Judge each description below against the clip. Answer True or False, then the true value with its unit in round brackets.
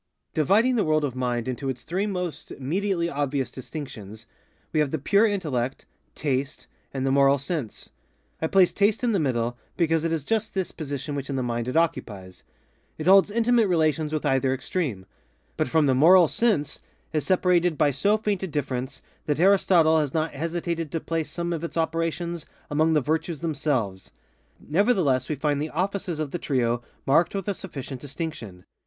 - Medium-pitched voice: True (155 Hz)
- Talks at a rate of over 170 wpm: True (180 wpm)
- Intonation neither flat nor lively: True (4.6 semitones)